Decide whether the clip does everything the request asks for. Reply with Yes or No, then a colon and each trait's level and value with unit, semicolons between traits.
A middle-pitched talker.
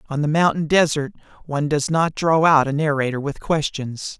Yes: medium, 150 Hz